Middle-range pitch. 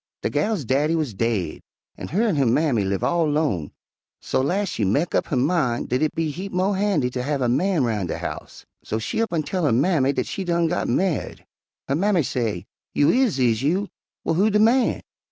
Yes: medium, 150 Hz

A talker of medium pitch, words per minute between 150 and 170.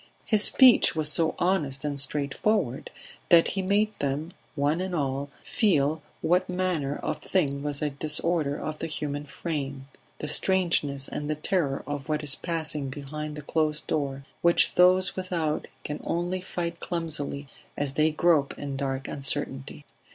Yes: medium, 150 Hz; average, 155 wpm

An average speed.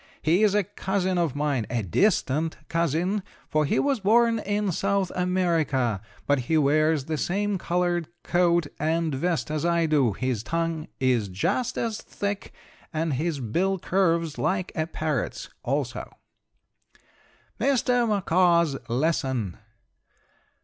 No: slow, 130 wpm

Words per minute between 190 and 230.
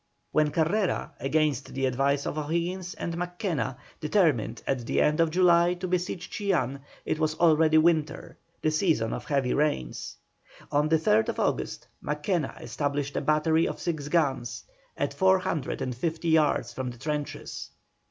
No: average, 155 wpm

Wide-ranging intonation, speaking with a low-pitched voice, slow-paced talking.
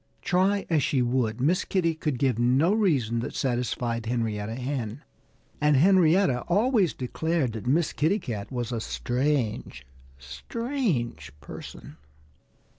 Yes: wide, 6.4 semitones; low, 130 Hz; slow, 125 wpm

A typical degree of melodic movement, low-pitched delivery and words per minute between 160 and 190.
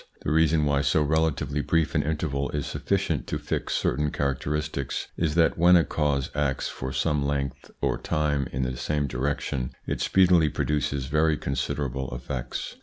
No: narrow, 2.0 semitones; very low, 75 Hz; average, 165 wpm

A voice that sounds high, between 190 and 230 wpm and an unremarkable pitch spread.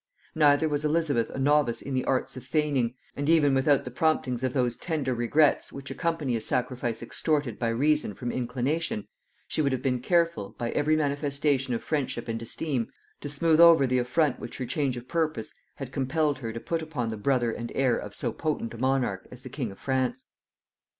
No: low, 135 Hz; average, 200 wpm; average, 3.8 semitones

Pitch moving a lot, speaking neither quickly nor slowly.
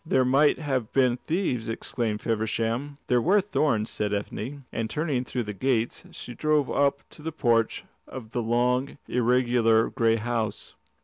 No: average, 3.6 semitones; average, 160 wpm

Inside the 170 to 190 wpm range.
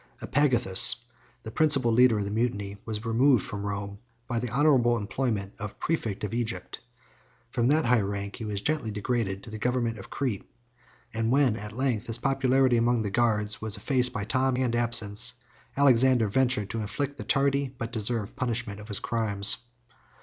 Yes: average, 175 wpm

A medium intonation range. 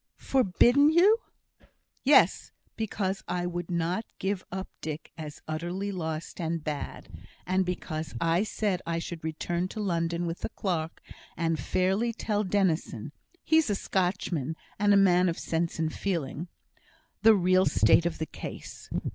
Yes: average, 3.3 semitones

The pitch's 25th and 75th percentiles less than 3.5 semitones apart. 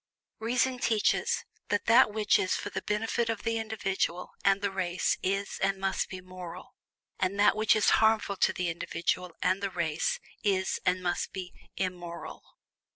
Yes: average, 2.9 semitones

